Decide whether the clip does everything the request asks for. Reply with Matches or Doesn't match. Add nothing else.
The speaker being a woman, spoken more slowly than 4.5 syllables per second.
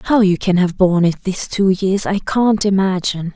Doesn't match